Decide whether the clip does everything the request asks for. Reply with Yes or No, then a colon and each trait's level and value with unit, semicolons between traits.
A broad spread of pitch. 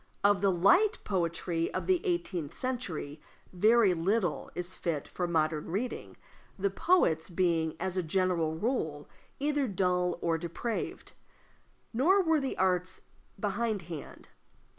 Yes: wide, 5.8 semitones